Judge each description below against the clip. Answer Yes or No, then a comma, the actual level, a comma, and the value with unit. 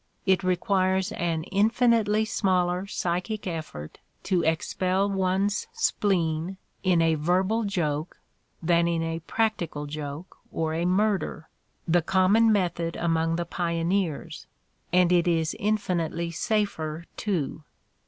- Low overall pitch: No, medium, 180 Hz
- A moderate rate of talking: No, slow, 115 wpm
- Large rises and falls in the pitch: No, average, 3.1 semitones